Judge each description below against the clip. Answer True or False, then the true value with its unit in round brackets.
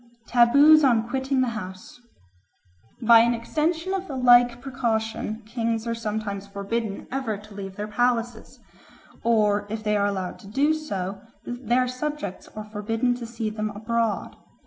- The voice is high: True (230 Hz)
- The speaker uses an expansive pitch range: False (2.9 semitones)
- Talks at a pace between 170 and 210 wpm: False (155 wpm)